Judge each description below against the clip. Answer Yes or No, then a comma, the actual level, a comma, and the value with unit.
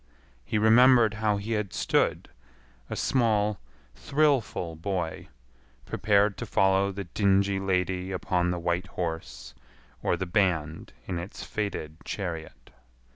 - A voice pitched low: Yes, very low, 95 Hz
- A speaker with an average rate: No, slow, 125 wpm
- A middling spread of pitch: Yes, average, 3.2 semitones